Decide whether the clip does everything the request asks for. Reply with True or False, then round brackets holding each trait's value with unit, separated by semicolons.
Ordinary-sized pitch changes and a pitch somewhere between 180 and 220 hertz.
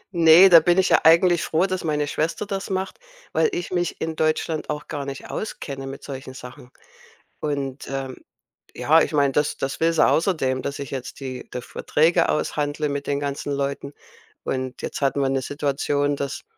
False (3.1 semitones; 145 Hz)